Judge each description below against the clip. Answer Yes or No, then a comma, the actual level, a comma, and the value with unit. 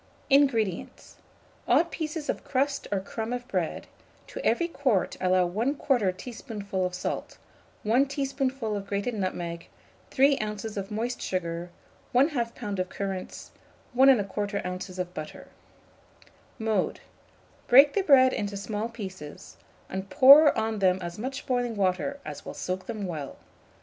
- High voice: Yes, high, 215 Hz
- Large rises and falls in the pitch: Yes, wide, 5.7 semitones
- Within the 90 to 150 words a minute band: Yes, average, 140 wpm